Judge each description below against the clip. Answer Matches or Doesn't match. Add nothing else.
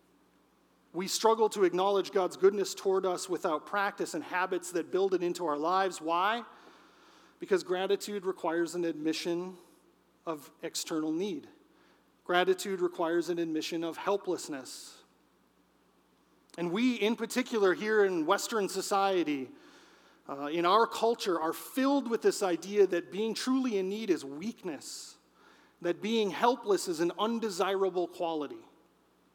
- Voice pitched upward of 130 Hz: Matches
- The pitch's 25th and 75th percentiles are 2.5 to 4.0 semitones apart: Doesn't match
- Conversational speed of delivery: Doesn't match